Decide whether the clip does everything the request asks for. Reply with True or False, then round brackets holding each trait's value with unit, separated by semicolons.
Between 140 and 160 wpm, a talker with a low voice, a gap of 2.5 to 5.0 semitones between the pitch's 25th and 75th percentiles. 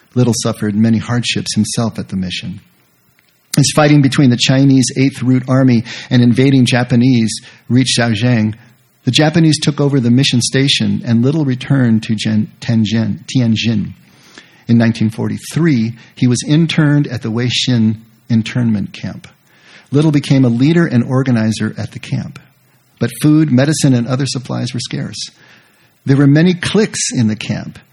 True (145 wpm; 125 Hz; 3.3 semitones)